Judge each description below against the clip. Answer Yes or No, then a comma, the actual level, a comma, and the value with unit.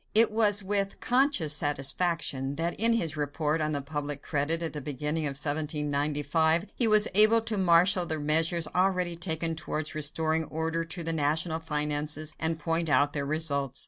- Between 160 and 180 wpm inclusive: Yes, average, 170 wpm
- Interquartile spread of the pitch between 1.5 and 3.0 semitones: Yes, average, 2.7 semitones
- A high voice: No, medium, 160 Hz